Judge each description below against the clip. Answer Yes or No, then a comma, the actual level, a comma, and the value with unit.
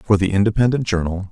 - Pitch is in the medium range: No, low, 100 Hz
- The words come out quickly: No, average, 180 wpm